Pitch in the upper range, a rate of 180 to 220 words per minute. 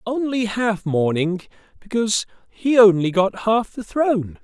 No: high, 210 Hz; slow, 135 wpm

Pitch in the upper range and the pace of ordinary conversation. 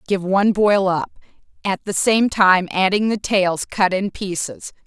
Yes: high, 195 Hz; average, 175 wpm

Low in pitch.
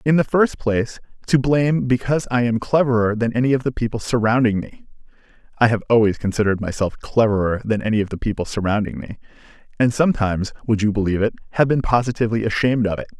Yes: low, 115 Hz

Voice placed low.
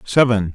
Yes: low, 110 Hz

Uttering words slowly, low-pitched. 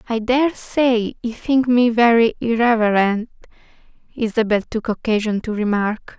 No: slow, 125 wpm; high, 230 Hz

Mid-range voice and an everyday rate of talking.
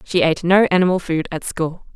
No: medium, 175 Hz; fast, 215 wpm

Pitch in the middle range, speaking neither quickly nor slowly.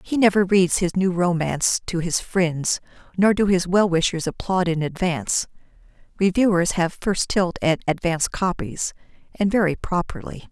Yes: medium, 180 Hz; average, 155 wpm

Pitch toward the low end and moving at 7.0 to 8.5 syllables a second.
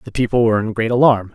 Yes: low, 115 Hz; 7.3 syllables/s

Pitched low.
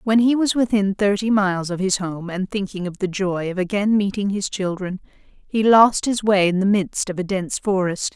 No: high, 195 Hz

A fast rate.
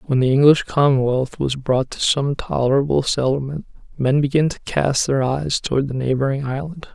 No: average, 175 wpm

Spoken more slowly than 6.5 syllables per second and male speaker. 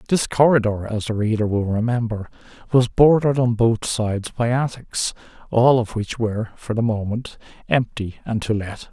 Yes: 5.0 syllables/s; male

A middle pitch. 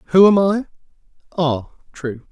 Yes: medium, 165 Hz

